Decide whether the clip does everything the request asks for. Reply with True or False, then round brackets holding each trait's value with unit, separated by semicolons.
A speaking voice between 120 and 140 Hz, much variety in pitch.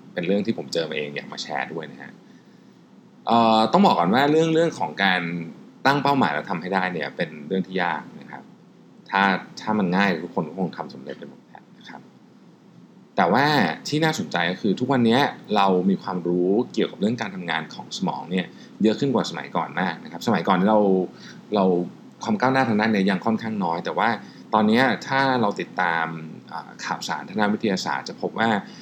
False (100 Hz; 5.7 semitones)